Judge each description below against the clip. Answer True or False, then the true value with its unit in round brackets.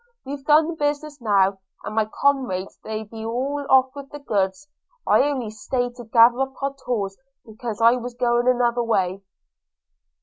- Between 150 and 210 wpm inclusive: True (175 wpm)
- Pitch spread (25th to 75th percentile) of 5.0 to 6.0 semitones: False (4.1 semitones)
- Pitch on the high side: True (245 Hz)